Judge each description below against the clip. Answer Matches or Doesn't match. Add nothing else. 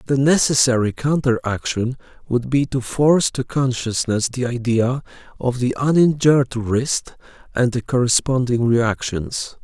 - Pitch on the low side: Matches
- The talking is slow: Matches